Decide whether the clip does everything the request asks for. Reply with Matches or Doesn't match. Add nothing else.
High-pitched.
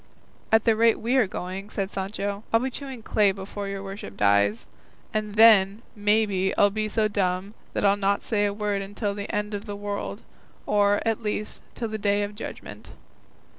Matches